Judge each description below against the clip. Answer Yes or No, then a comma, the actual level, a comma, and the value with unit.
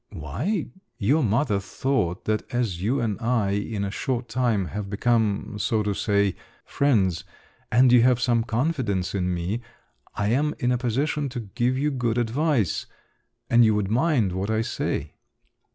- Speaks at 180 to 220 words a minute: No, average, 160 wpm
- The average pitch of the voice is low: Yes, low, 115 Hz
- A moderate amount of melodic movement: Yes, average, 4.0 semitones